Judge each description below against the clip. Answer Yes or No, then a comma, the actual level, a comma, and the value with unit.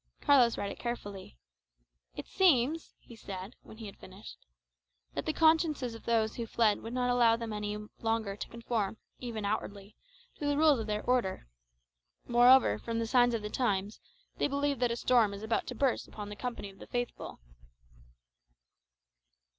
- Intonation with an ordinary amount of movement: Yes, average, 3.0 semitones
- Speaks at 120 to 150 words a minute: No, average, 175 wpm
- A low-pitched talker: No, high, 230 Hz